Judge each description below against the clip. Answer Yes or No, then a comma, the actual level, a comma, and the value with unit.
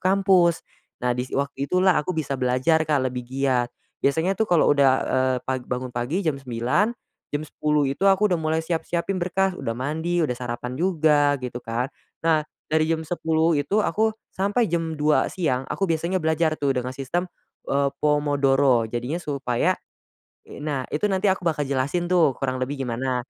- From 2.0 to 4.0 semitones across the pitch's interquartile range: No, average, 4.7 semitones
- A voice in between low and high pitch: Yes, medium, 150 Hz